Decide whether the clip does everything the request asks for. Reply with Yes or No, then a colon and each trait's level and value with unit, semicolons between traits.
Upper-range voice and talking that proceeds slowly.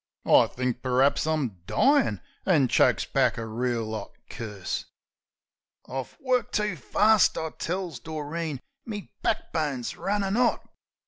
No: medium, 150 Hz; slow, 130 wpm